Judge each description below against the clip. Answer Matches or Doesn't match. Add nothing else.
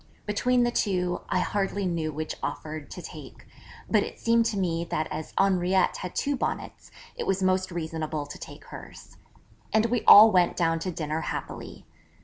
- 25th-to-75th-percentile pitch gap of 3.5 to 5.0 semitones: Matches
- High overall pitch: Doesn't match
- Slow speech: Doesn't match